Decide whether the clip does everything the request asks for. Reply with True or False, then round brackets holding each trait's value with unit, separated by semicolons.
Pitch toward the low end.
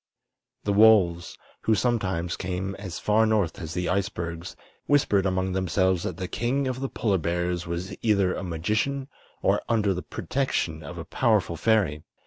True (95 Hz)